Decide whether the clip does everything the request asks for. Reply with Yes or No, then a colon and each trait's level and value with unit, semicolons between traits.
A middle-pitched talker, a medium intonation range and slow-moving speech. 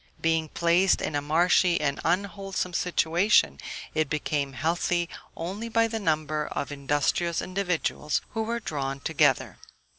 Yes: medium, 165 Hz; average, 3.7 semitones; slow, 130 wpm